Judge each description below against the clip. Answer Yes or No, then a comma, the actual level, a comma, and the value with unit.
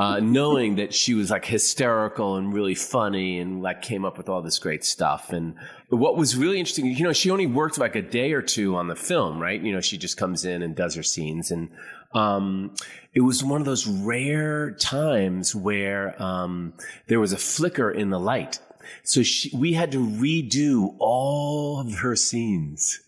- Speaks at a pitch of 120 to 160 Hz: No, low, 105 Hz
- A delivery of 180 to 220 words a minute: Yes, average, 200 wpm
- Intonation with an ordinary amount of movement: No, wide, 6.4 semitones